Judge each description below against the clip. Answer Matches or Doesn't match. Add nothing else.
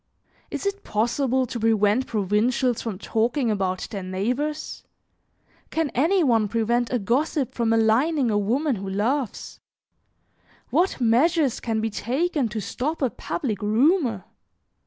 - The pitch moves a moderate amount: Matches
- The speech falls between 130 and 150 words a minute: Matches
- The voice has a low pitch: Doesn't match